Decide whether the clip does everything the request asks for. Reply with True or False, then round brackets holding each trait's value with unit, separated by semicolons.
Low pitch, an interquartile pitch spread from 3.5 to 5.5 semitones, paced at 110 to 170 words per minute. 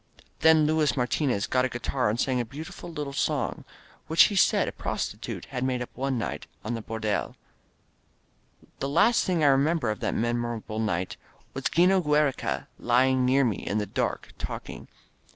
False (130 Hz; 4.2 semitones; 180 wpm)